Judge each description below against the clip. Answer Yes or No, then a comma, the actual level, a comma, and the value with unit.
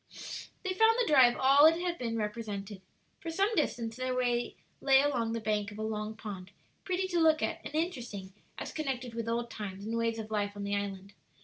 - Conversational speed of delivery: No, fast, 210 wpm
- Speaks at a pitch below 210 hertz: No, high, 230 Hz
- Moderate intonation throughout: No, wide, 6.4 semitones